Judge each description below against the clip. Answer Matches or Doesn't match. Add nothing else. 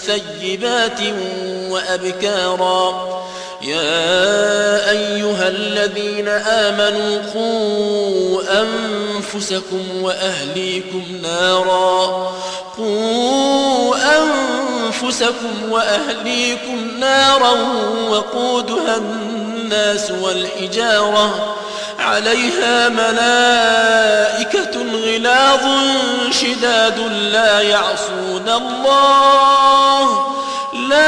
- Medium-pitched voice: Doesn't match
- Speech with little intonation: Doesn't match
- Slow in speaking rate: Matches